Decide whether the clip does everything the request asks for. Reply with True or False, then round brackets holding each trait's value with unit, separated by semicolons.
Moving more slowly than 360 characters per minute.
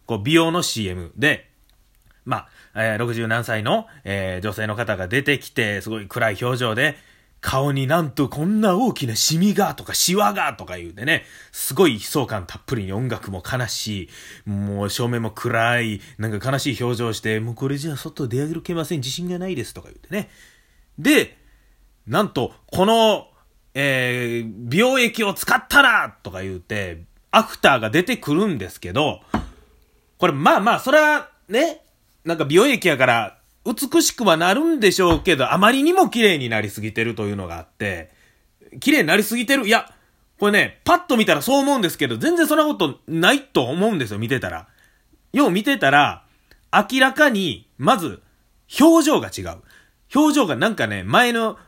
True (325 characters per minute)